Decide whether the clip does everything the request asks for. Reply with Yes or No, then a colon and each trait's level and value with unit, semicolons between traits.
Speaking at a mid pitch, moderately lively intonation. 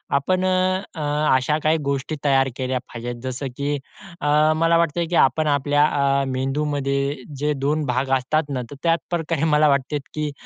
No: medium, 145 Hz; narrow, 2.3 semitones